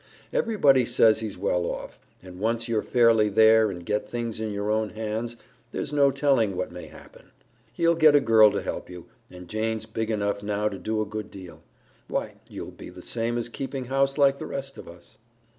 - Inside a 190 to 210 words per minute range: Yes, fast, 205 wpm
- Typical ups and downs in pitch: Yes, average, 3.3 semitones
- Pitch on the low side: Yes, low, 110 Hz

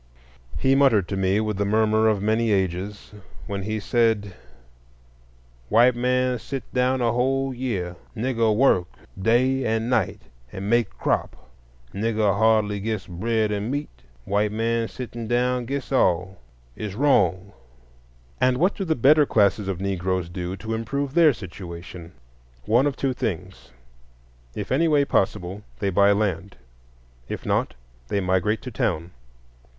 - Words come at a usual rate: Yes, average, 145 wpm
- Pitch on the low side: Yes, low, 110 Hz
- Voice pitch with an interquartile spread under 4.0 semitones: No, average, 4.4 semitones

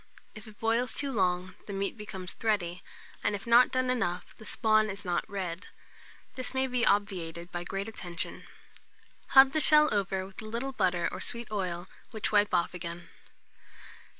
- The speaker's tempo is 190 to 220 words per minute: No, average, 175 wpm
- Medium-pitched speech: No, high, 205 Hz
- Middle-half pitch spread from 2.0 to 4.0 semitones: No, average, 4.4 semitones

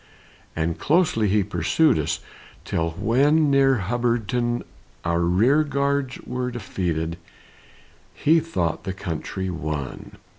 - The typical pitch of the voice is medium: No, low, 115 Hz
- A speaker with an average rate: No, slow, 110 wpm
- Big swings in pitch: Yes, wide, 8.3 semitones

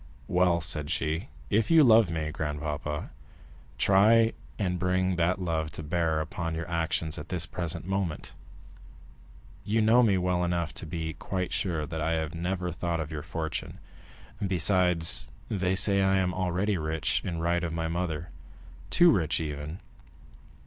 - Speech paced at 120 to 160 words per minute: Yes, average, 155 wpm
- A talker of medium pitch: No, very low, 85 Hz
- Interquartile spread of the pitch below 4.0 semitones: Yes, narrow, 2.6 semitones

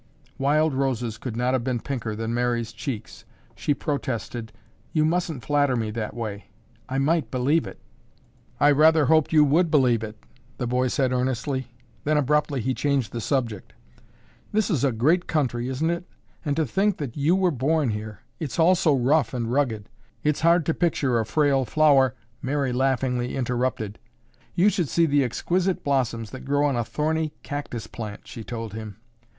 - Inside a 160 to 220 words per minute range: Yes, average, 175 wpm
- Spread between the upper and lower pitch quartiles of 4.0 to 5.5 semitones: Yes, average, 4.3 semitones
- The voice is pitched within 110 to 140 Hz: Yes, low, 135 Hz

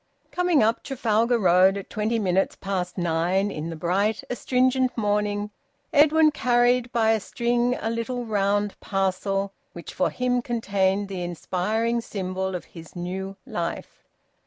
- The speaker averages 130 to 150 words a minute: Yes, average, 140 wpm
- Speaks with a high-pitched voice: Yes, high, 205 Hz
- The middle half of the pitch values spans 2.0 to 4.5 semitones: Yes, average, 4.1 semitones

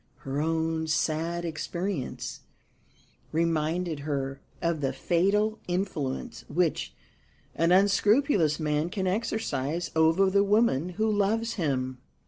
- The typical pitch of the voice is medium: Yes, medium, 170 Hz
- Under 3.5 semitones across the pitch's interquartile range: No, average, 4.5 semitones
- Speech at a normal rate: No, slow, 110 wpm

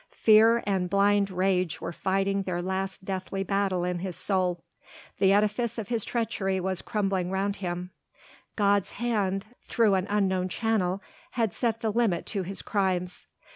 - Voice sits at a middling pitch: No, high, 195 Hz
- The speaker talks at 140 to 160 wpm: Yes, average, 155 wpm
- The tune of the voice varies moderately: No, narrow, 2.0 semitones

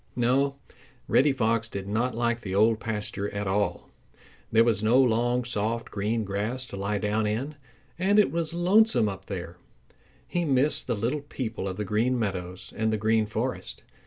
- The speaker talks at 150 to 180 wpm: Yes, average, 175 wpm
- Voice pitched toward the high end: No, low, 115 Hz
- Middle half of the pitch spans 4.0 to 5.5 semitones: No, average, 3.6 semitones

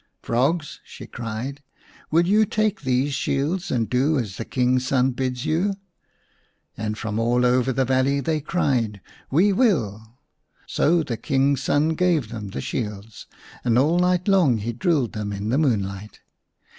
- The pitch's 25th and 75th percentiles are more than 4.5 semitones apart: Yes, wide, 5.6 semitones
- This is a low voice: Yes, low, 130 Hz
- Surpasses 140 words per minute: Yes, average, 170 wpm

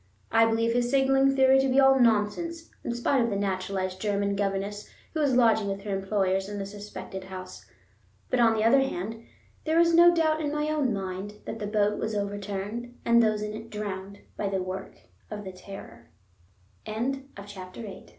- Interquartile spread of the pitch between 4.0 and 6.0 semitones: Yes, average, 4.8 semitones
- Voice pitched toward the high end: Yes, high, 215 Hz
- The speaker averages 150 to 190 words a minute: Yes, average, 170 wpm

